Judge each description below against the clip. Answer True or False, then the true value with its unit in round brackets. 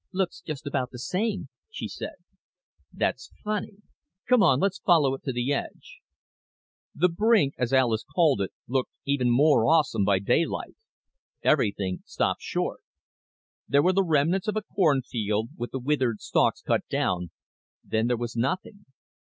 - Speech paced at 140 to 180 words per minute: True (155 wpm)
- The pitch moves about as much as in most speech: False (7.3 semitones)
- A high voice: False (140 Hz)